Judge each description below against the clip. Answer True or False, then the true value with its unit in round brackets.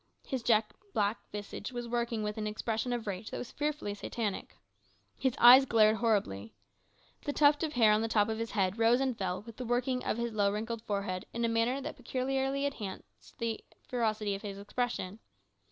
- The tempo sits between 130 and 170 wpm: False (195 wpm)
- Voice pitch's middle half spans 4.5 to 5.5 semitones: False (2.8 semitones)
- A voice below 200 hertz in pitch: False (225 Hz)